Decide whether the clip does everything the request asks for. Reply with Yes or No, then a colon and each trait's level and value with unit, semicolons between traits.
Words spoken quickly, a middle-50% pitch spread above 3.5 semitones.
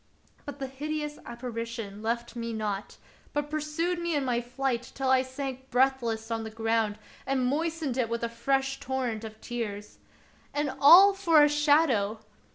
No: average, 165 wpm; average, 4.1 semitones